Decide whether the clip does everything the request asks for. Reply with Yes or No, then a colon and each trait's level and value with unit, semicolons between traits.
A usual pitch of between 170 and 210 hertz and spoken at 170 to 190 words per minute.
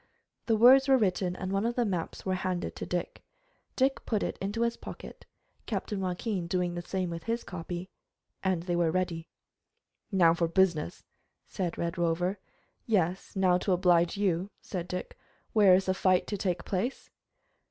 Yes: medium, 185 Hz; average, 175 wpm